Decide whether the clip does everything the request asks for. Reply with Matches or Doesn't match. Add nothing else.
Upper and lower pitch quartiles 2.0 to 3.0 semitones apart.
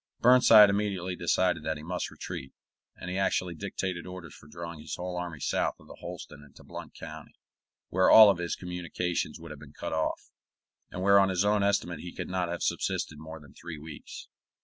Matches